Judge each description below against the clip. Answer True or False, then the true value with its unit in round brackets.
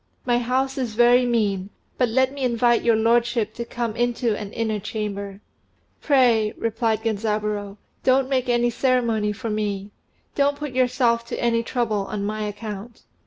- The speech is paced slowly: False (160 wpm)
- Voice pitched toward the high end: True (230 Hz)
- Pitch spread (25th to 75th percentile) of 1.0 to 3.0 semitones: True (2.6 semitones)